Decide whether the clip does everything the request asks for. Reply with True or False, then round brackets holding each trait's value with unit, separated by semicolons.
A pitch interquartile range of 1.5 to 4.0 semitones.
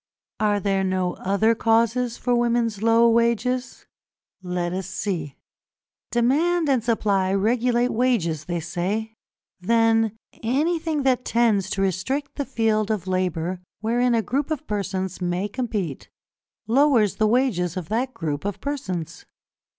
False (4.5 semitones)